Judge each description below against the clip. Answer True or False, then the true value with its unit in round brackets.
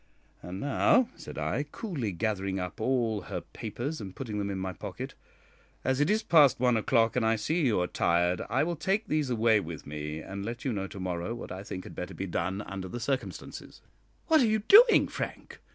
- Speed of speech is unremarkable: False (215 wpm)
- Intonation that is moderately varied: False (6.7 semitones)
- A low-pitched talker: True (110 Hz)